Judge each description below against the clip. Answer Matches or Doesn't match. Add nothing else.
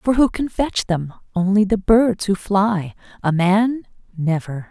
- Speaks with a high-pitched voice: Matches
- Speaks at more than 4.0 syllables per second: Doesn't match